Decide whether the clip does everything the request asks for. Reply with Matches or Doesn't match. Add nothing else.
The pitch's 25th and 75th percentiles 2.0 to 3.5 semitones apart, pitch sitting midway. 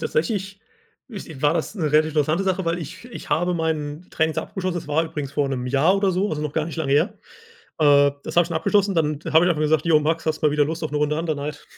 Matches